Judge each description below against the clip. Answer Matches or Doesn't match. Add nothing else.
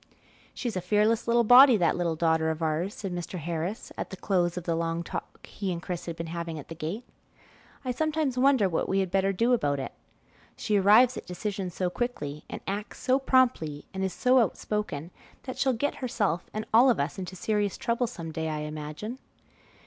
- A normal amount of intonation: Doesn't match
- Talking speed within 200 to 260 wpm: Matches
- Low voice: Doesn't match